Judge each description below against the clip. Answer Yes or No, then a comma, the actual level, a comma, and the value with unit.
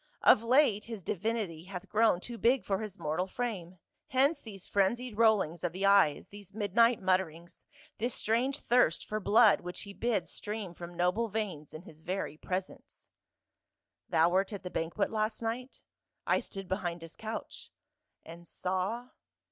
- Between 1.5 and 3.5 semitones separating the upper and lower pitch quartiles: No, average, 4.1 semitones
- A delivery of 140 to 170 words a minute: Yes, average, 165 wpm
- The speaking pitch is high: Yes, high, 200 Hz